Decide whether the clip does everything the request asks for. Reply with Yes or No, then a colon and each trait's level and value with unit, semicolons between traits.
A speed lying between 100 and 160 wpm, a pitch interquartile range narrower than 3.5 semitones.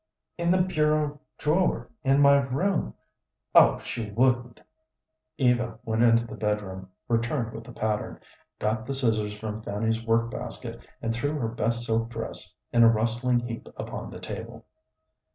Yes: average, 150 wpm; average, 3.1 semitones